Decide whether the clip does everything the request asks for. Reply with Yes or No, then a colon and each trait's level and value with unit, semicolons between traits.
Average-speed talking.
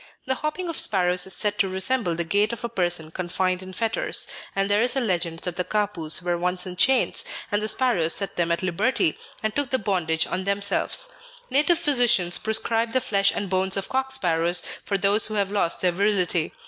No: fast, 210 wpm